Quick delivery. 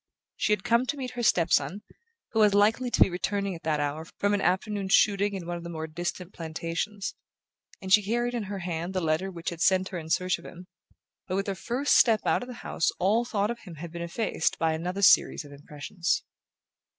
Yes: fast, 230 wpm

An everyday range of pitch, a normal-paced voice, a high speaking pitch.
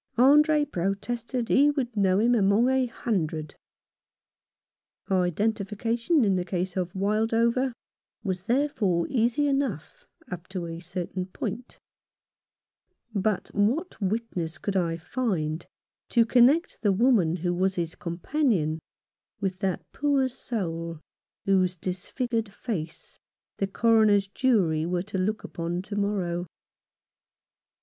No: average, 5.0 semitones; slow, 115 wpm; high, 200 Hz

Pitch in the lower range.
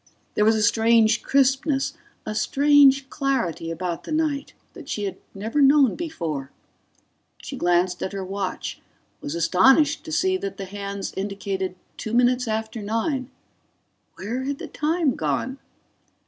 No: high, 225 Hz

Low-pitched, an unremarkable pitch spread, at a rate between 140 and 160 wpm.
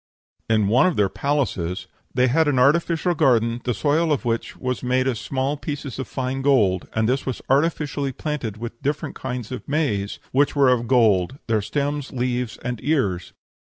No: low, 130 Hz; average, 3.7 semitones; average, 180 wpm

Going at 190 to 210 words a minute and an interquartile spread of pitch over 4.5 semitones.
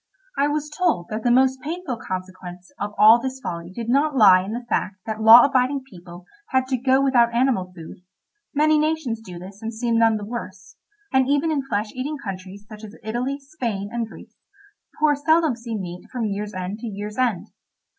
Yes: average, 195 wpm; average, 5.0 semitones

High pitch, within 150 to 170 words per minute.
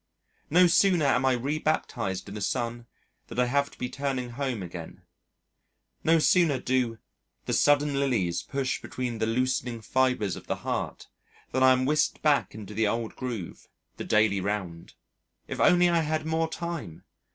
No: low, 130 Hz; average, 165 wpm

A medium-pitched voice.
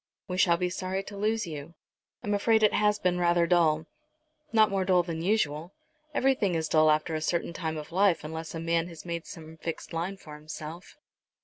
Yes: medium, 170 Hz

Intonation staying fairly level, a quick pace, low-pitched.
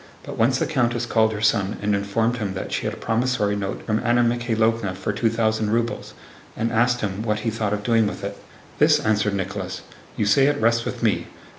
Yes: narrow, 2.3 semitones; fast, 220 wpm; low, 110 Hz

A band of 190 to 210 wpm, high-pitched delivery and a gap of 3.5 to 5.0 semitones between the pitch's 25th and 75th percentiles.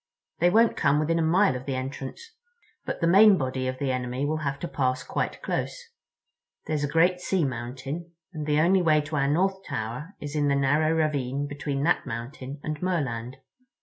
No: average, 195 wpm; medium, 145 Hz; average, 4.0 semitones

